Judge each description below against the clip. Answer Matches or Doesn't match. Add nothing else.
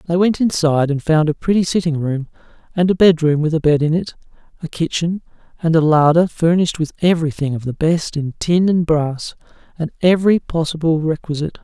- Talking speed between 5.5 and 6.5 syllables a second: Matches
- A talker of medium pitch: Matches